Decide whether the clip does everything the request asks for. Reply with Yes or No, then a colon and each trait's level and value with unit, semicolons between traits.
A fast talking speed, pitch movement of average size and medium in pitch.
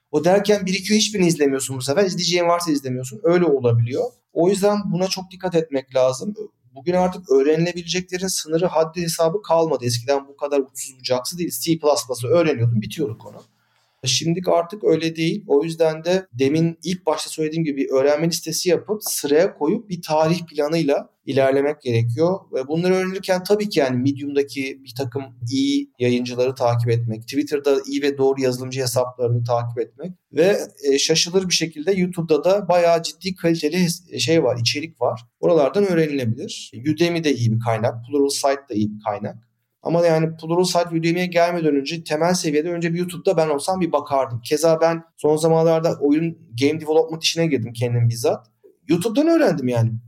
Yes: fast, 165 wpm; average, 4.4 semitones; medium, 155 Hz